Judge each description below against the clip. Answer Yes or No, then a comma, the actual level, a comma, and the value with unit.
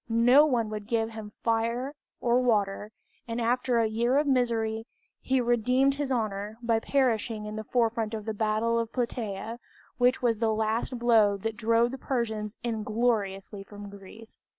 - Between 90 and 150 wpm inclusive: No, average, 165 wpm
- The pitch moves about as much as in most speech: No, narrow, 2.1 semitones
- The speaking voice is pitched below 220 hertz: No, high, 225 Hz